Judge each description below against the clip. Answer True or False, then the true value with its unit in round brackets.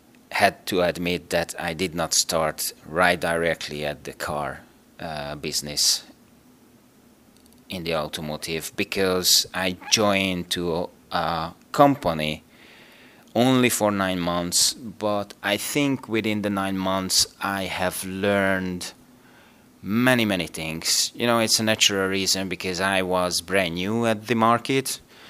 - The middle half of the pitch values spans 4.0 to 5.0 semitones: False (3.4 semitones)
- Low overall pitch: True (95 Hz)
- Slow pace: True (130 wpm)